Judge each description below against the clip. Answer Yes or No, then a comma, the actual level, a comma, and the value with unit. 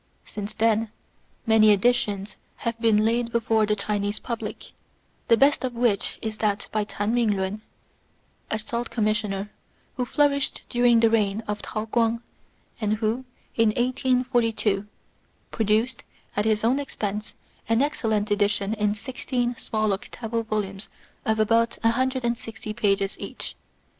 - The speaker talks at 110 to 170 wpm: Yes, slow, 135 wpm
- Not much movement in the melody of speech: Yes, narrow, 2.1 semitones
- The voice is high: Yes, high, 220 Hz